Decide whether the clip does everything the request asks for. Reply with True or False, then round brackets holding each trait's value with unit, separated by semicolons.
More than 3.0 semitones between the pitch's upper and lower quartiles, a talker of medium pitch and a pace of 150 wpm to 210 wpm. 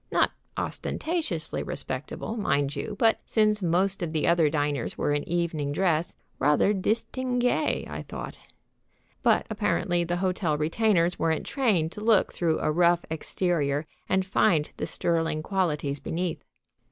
False (4.1 semitones; 170 Hz; 140 wpm)